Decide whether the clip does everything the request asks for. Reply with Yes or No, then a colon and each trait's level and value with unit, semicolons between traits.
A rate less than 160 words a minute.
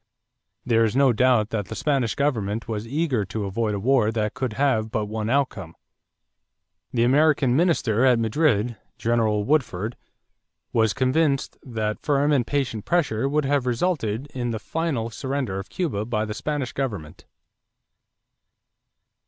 Yes: average, 145 wpm